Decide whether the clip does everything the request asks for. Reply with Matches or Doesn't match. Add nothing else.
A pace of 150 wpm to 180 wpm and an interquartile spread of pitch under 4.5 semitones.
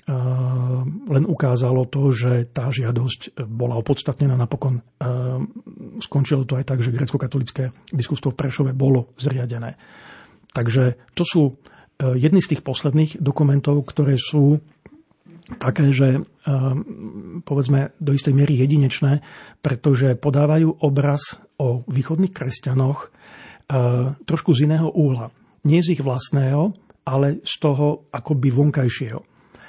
Doesn't match